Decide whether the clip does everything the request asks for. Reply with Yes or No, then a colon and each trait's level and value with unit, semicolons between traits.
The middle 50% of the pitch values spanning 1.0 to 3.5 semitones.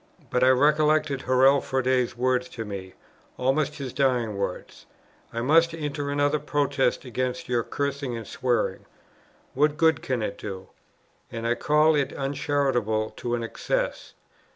Yes: average, 3.2 semitones